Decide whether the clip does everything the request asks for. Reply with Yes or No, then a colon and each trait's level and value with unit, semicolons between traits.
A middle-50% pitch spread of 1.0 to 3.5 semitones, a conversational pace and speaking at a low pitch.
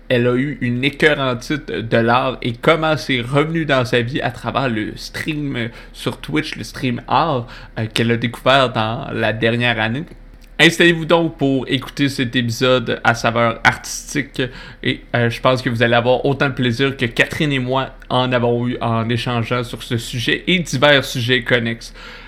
Yes: average, 2.8 semitones; average, 180 wpm; low, 125 Hz